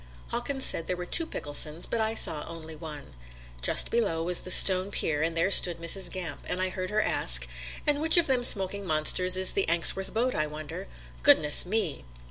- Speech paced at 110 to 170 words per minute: No, fast, 205 wpm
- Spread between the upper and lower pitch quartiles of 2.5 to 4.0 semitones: No, average, 4.7 semitones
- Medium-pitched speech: Yes, medium, 180 Hz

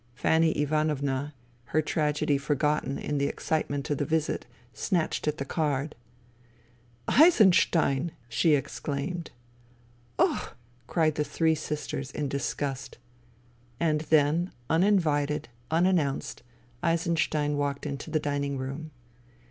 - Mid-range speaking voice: Yes, medium, 150 Hz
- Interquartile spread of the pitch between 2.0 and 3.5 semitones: Yes, narrow, 2.4 semitones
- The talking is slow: Yes, slow, 120 wpm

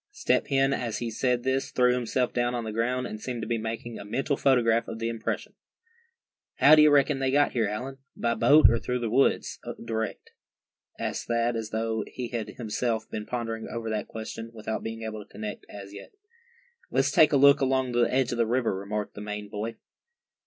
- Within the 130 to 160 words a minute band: No, fast, 205 wpm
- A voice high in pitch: No, low, 115 Hz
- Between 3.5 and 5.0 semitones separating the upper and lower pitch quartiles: No, narrow, 2.5 semitones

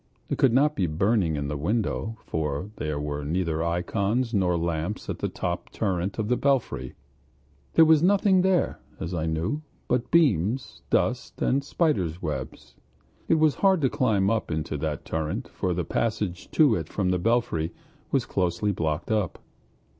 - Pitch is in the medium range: No, very low, 95 Hz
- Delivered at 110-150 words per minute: No, average, 170 wpm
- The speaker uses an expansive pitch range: Yes, wide, 7.3 semitones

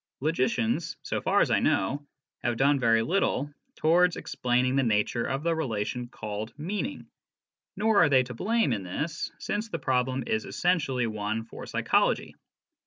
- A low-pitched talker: Yes, low, 130 Hz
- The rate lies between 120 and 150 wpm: No, average, 165 wpm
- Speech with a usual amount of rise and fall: No, wide, 6.1 semitones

